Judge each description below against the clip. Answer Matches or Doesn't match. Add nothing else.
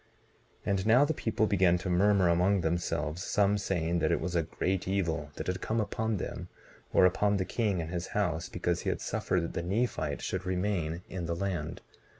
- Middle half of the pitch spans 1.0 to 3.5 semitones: Matches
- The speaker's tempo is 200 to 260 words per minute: Matches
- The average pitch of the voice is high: Doesn't match